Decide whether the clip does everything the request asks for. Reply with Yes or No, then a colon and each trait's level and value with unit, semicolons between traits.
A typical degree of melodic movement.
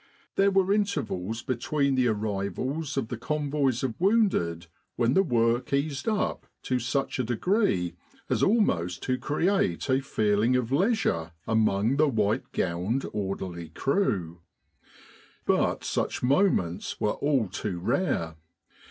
No: wide, 7.2 semitones